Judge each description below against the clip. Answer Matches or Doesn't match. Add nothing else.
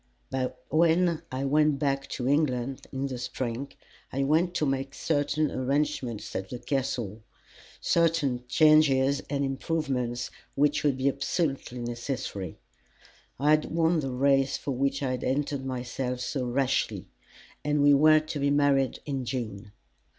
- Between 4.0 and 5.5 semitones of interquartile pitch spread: Doesn't match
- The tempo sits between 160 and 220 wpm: Doesn't match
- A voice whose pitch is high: Doesn't match